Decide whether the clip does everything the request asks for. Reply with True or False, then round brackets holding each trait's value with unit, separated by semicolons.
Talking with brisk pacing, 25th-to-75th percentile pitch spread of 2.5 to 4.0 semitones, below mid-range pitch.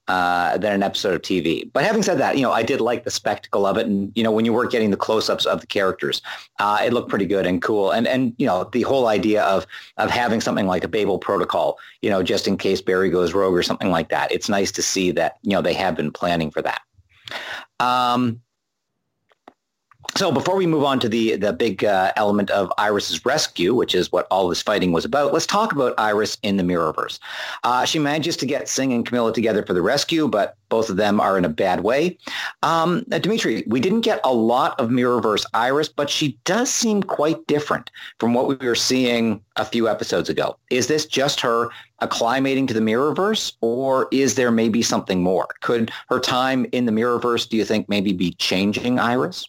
True (220 wpm; 3.7 semitones; 120 Hz)